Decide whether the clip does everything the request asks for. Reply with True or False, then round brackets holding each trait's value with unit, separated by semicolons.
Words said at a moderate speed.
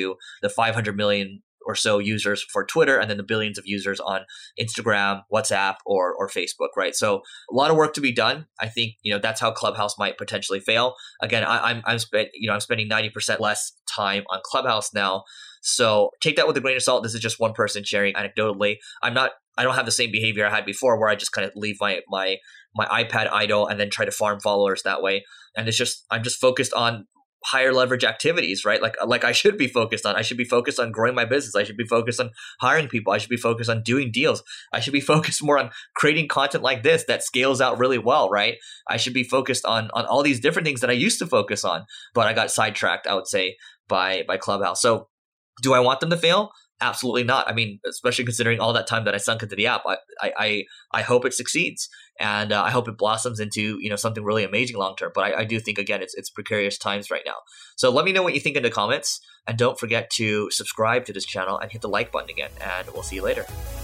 False (250 wpm)